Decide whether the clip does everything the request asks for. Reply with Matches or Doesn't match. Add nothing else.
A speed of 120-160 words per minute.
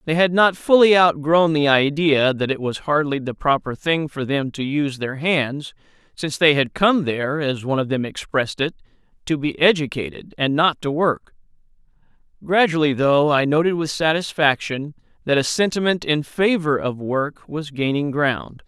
Doesn't match